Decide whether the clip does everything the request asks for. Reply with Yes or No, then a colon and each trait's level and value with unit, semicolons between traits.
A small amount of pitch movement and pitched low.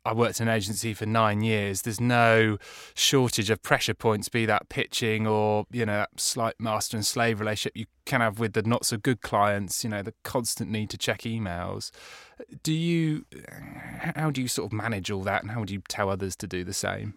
Yes: narrow, 2.0 semitones; low, 110 Hz